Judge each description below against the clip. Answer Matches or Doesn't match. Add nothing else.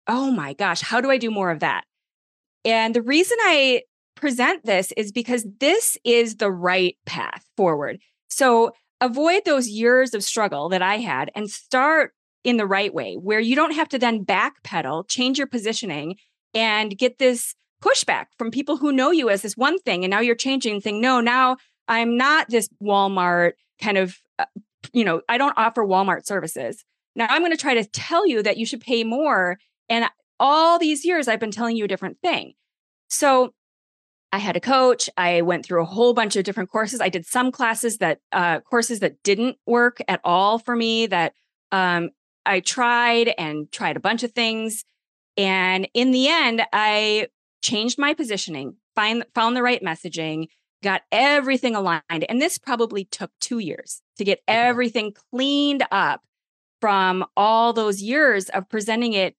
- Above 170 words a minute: Matches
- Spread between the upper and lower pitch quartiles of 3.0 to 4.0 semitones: Doesn't match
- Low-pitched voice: Doesn't match